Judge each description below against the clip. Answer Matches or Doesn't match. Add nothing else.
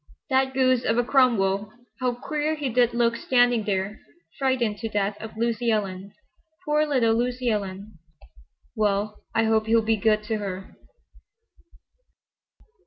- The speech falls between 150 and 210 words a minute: Doesn't match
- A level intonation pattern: Doesn't match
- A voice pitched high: Matches